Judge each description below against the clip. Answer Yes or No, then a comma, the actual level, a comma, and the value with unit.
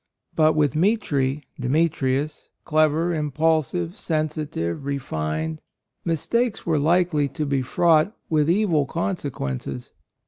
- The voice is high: No, medium, 155 Hz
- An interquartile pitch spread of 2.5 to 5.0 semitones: Yes, average, 3.4 semitones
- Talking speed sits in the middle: No, slow, 115 wpm